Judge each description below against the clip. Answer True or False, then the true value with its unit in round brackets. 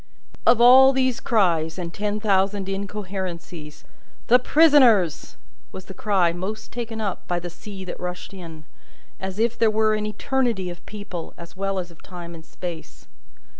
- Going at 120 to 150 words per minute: False (165 wpm)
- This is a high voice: True (195 Hz)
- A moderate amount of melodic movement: True (3.7 semitones)